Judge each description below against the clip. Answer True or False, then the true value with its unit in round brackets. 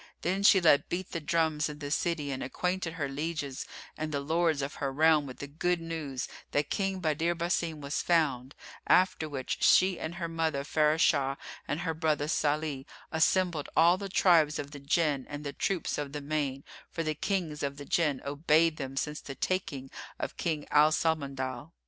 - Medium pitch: True (155 Hz)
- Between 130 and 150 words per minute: False (185 wpm)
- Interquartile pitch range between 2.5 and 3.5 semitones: True (2.8 semitones)